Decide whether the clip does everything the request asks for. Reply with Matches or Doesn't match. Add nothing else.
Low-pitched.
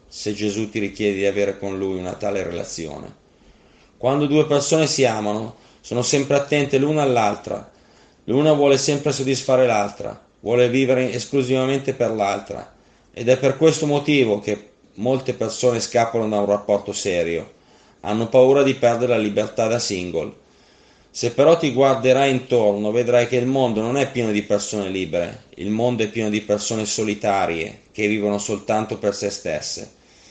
Matches